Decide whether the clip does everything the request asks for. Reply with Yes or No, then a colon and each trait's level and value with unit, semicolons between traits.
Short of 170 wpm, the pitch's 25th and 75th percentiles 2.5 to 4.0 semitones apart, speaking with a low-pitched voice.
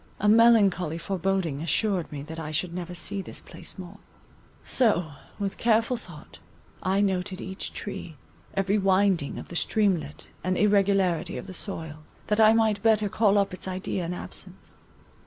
No: average, 160 wpm; average, 3.0 semitones; high, 190 Hz